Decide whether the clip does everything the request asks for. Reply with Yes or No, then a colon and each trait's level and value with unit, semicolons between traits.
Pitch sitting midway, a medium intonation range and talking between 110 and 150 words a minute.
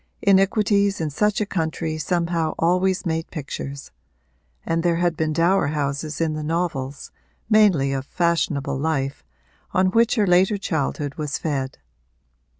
Yes: medium, 165 Hz; average, 4.0 semitones; average, 140 wpm